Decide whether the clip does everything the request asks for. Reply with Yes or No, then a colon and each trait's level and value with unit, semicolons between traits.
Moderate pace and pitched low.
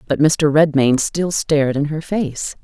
No: average, 180 wpm; medium, 150 Hz